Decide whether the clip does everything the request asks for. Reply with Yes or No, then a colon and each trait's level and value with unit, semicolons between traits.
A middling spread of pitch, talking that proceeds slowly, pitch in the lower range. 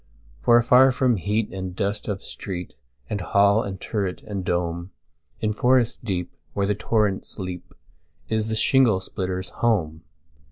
Yes: average, 3.5 semitones; slow, 130 wpm; low, 100 Hz